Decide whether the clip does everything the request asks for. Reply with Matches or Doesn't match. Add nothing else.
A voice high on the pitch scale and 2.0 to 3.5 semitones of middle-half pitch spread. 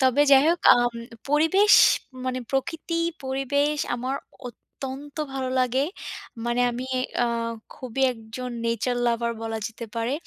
Matches